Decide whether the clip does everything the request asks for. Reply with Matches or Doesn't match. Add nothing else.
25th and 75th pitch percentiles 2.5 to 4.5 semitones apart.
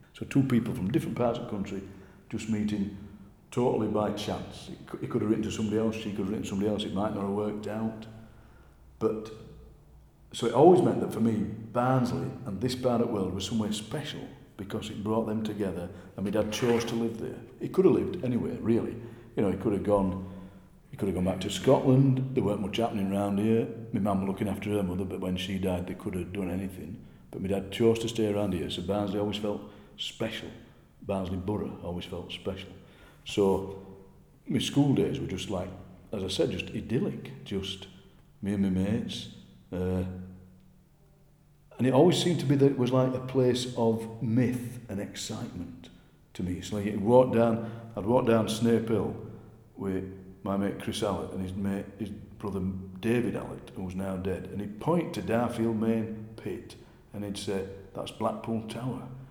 Matches